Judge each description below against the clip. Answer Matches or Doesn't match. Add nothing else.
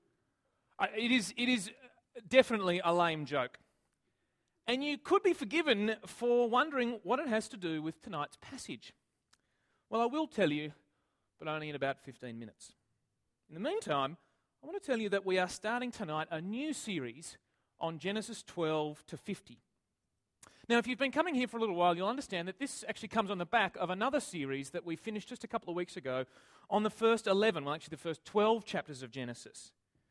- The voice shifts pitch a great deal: Matches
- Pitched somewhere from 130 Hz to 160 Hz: Doesn't match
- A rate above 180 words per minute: Matches